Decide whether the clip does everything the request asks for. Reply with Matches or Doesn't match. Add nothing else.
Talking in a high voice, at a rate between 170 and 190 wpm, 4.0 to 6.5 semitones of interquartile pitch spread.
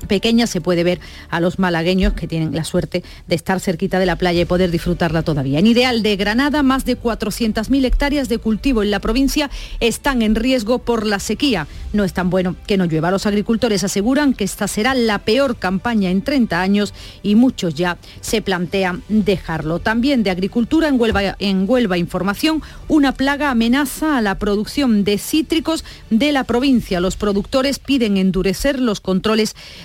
Matches